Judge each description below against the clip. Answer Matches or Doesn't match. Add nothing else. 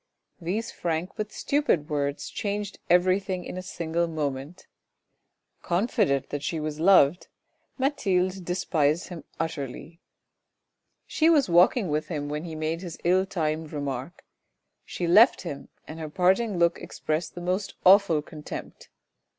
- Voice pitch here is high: Doesn't match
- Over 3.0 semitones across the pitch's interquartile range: Matches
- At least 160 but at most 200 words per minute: Doesn't match